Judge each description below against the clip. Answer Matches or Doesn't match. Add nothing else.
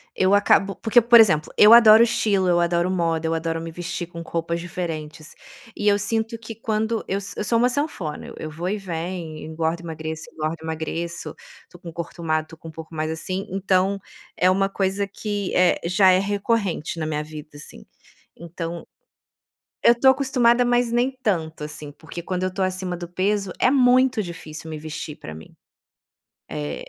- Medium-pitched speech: Matches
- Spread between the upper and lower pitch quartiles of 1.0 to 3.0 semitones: Doesn't match